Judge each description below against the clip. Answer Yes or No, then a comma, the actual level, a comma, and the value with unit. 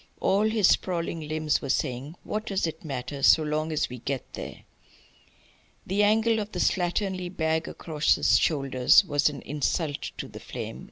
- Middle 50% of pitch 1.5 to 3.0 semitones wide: No, average, 4.6 semitones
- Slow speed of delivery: No, average, 170 wpm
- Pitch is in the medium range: Yes, medium, 160 Hz